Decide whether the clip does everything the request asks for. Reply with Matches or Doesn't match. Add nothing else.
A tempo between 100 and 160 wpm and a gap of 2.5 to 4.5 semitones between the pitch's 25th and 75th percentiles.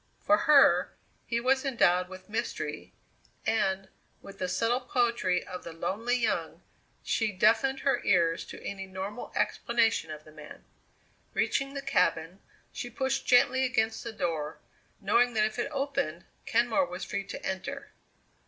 Doesn't match